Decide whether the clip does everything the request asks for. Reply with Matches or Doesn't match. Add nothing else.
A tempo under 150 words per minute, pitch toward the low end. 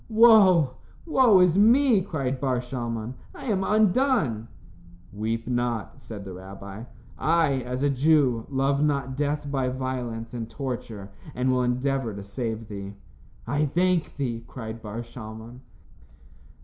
Matches